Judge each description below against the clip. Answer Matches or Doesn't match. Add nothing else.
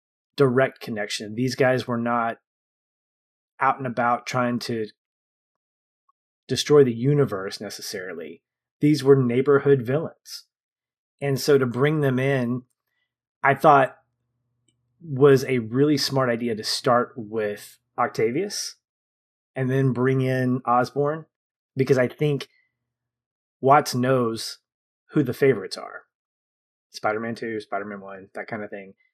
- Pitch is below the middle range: Matches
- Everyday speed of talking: Doesn't match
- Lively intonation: Doesn't match